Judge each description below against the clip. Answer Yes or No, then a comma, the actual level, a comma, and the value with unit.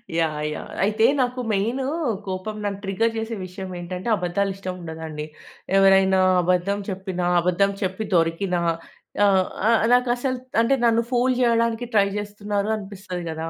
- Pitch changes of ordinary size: Yes, average, 3.7 semitones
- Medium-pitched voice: No, high, 195 Hz